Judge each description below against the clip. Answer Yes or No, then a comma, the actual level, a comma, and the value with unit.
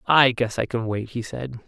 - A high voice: No, low, 120 Hz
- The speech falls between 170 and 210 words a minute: No, fast, 250 wpm